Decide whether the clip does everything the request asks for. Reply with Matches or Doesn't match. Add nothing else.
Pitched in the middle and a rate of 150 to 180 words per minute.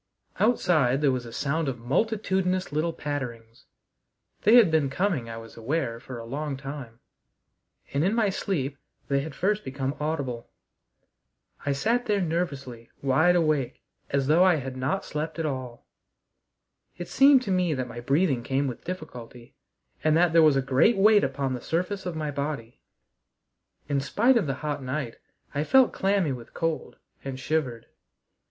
Matches